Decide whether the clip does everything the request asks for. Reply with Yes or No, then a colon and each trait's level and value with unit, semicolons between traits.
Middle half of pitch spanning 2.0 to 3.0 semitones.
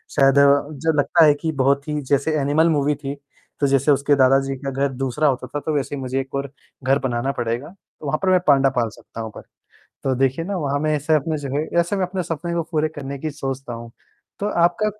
Yes: narrow, 2.5 semitones